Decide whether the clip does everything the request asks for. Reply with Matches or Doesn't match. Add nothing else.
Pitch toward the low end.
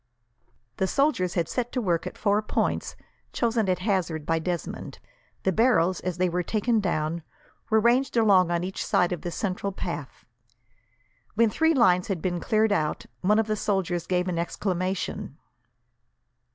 Doesn't match